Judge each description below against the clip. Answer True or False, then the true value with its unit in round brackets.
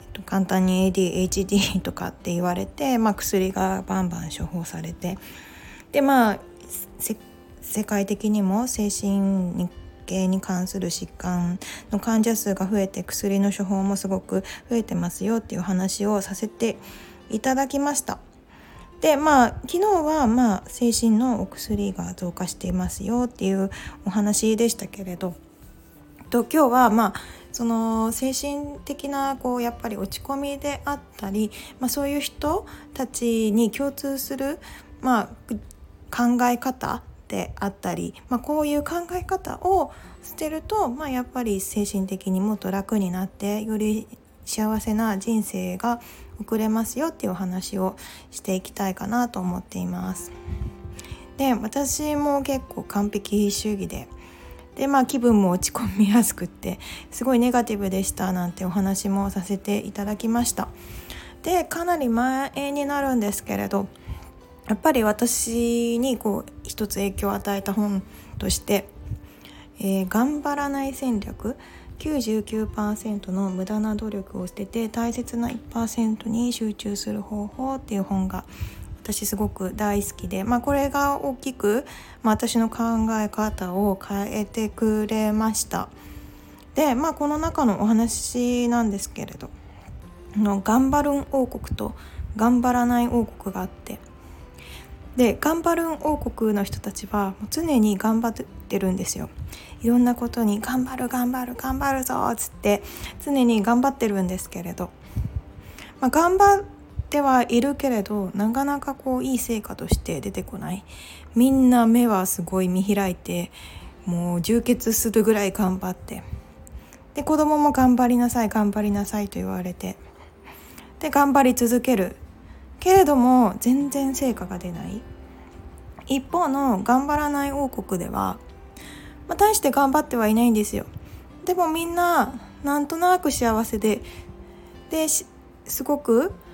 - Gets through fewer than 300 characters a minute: True (275 characters per minute)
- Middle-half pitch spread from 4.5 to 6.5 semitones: True (5.1 semitones)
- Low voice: False (220 Hz)